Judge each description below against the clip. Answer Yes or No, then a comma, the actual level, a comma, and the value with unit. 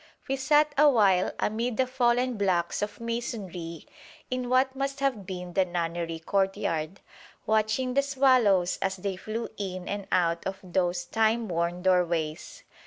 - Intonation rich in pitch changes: Yes, wide, 5.7 semitones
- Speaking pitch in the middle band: No, high, 200 Hz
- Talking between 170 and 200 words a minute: No, average, 140 wpm